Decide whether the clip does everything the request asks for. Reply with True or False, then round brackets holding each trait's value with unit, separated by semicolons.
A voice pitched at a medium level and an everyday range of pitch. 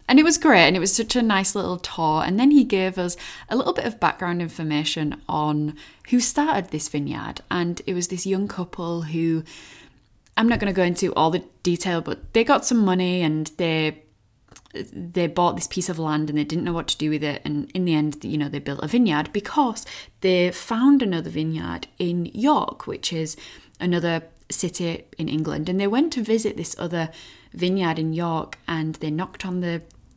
True (175 Hz; 3.6 semitones)